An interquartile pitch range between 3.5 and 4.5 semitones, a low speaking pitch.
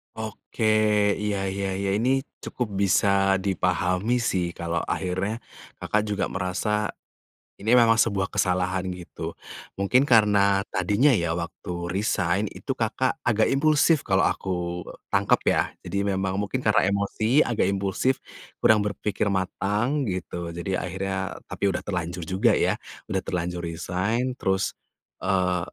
No: average, 2.9 semitones; low, 100 Hz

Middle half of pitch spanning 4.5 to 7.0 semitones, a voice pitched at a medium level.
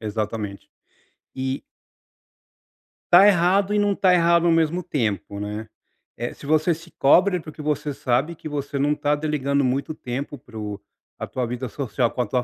Yes: wide, 5.4 semitones; medium, 145 Hz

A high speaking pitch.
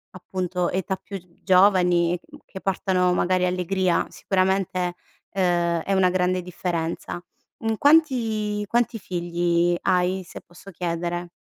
No: medium, 180 Hz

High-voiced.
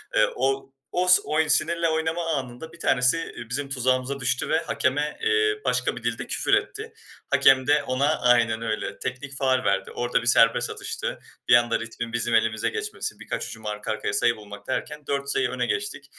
No: low, 130 Hz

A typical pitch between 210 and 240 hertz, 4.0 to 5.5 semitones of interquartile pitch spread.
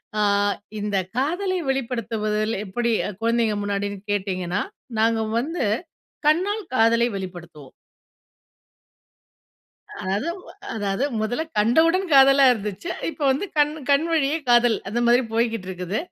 Yes: high, 230 Hz; average, 5.1 semitones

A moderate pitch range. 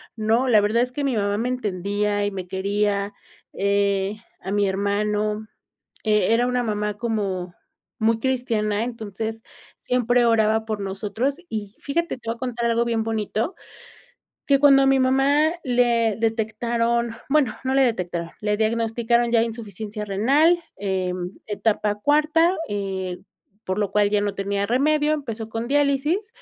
Yes: average, 3.3 semitones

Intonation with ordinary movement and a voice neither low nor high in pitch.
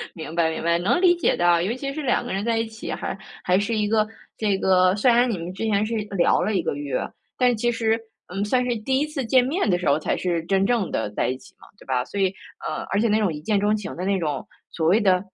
No: average, 4.7 semitones; high, 205 Hz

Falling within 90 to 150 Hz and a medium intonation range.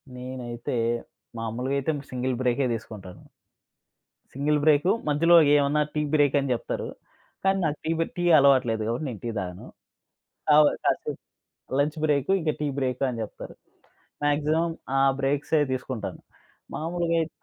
Yes: medium, 140 Hz; average, 3.4 semitones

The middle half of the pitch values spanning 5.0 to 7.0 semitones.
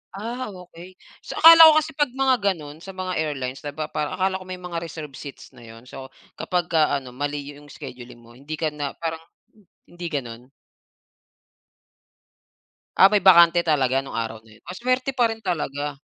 Yes: average, 5.3 semitones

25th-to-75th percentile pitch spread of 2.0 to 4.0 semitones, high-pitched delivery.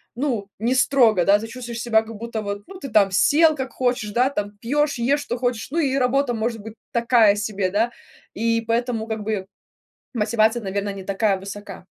Yes: average, 3.2 semitones; high, 230 Hz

